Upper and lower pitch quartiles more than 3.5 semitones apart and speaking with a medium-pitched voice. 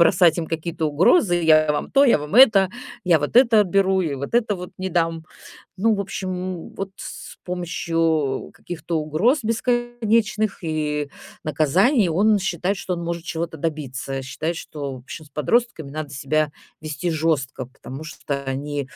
Yes: average, 4.5 semitones; medium, 165 Hz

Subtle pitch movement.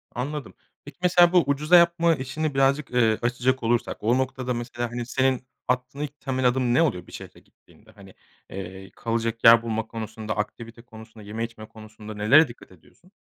No: average, 3.5 semitones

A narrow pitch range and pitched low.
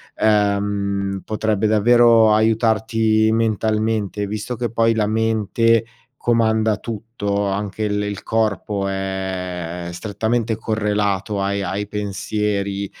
Yes: narrow, 1.9 semitones; low, 105 Hz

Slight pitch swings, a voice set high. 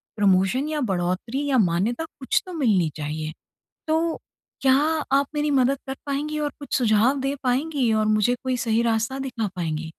No: average, 5.2 semitones; high, 245 Hz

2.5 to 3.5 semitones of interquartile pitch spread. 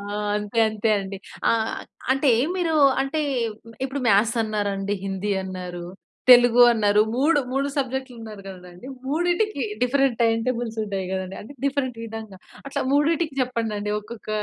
No: average, 4.9 semitones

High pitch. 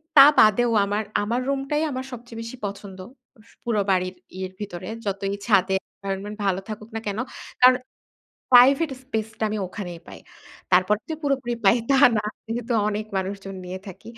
Yes: high, 210 Hz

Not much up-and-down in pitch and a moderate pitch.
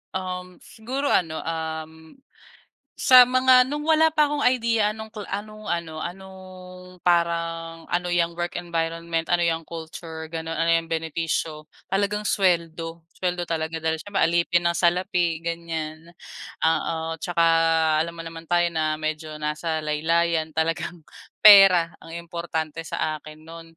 Yes: narrow, 2.0 semitones; medium, 170 Hz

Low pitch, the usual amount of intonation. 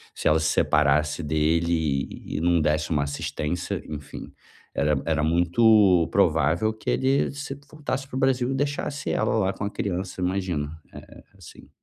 No: very low, 85 Hz; wide, 6.3 semitones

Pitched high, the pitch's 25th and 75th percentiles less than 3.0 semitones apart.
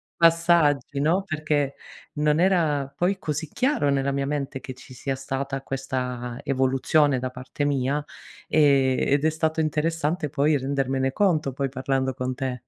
No: medium, 140 Hz; narrow, 2.6 semitones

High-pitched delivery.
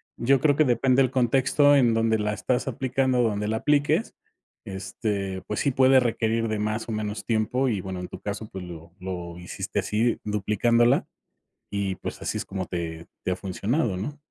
No: low, 110 Hz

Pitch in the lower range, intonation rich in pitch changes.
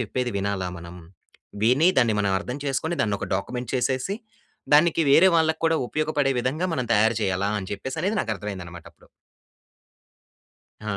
Yes: low, 125 Hz; wide, 7.2 semitones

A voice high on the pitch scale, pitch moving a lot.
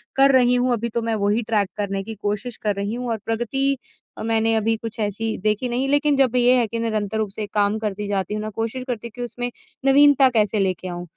No: high, 225 Hz; average, 2.9 semitones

